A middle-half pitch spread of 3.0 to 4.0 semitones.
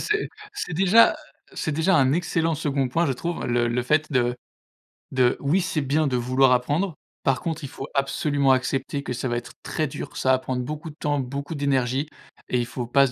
Yes: average, 3.6 semitones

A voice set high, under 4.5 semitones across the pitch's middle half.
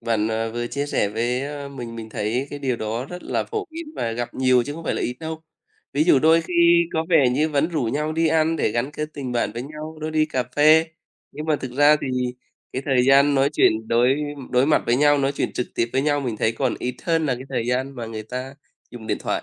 No: low, 135 Hz; average, 4.0 semitones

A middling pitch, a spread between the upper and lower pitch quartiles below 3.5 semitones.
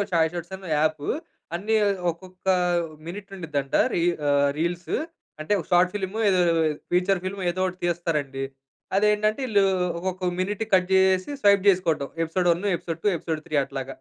Yes: medium, 180 Hz; average, 2.8 semitones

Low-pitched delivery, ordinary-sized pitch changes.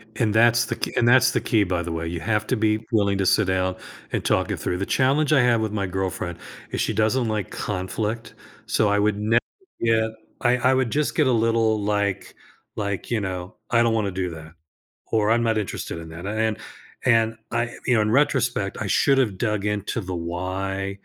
Yes: low, 110 Hz; average, 3.3 semitones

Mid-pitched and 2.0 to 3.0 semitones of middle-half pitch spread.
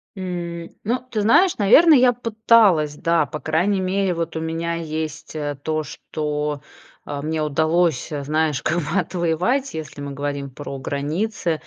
No: medium, 160 Hz; average, 4.2 semitones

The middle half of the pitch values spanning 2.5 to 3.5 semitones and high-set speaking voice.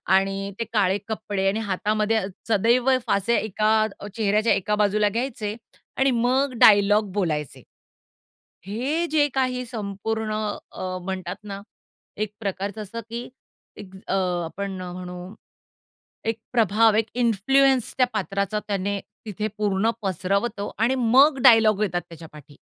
Yes: average, 2.8 semitones; high, 210 Hz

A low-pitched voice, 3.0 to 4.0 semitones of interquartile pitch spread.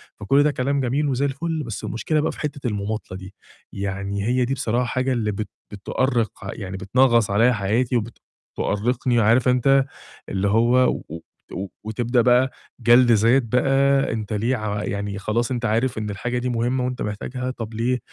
Yes: low, 120 Hz; average, 3.4 semitones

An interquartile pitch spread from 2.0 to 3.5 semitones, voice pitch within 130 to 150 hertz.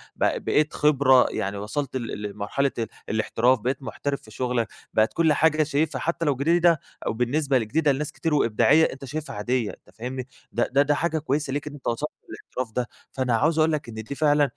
No: average, 4.0 semitones; low, 135 Hz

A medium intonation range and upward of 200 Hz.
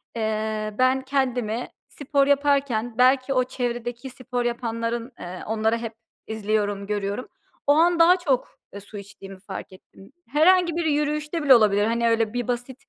Yes: average, 4.1 semitones; high, 240 Hz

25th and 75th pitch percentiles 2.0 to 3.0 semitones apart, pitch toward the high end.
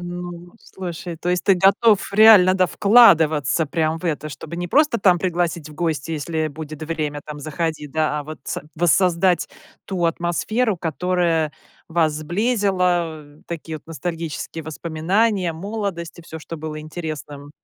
No: narrow, 2.6 semitones; medium, 170 Hz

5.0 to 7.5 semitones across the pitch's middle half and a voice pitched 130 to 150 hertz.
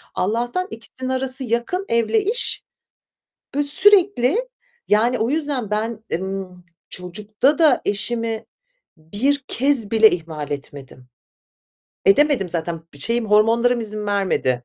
No: wide, 5.4 semitones; high, 230 Hz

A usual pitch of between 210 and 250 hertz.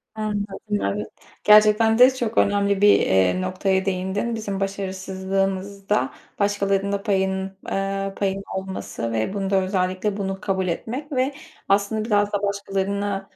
No: high, 195 Hz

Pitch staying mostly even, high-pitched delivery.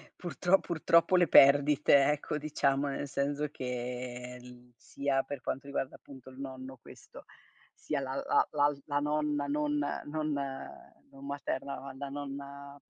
No: narrow, 1.6 semitones; medium, 140 Hz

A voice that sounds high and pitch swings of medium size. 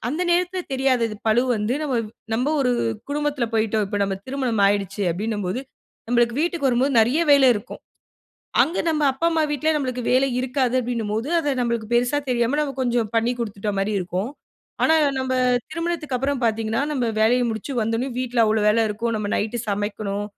Yes: high, 240 Hz; average, 4.0 semitones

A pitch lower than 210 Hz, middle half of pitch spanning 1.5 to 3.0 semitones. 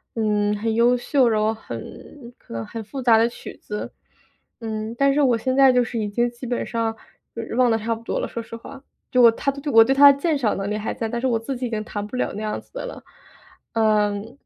No: high, 230 Hz; narrow, 2.5 semitones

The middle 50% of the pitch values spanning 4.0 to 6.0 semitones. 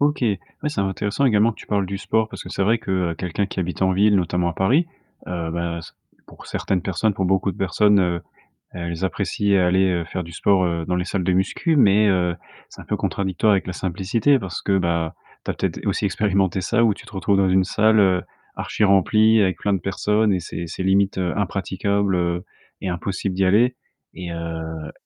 No: narrow, 2.5 semitones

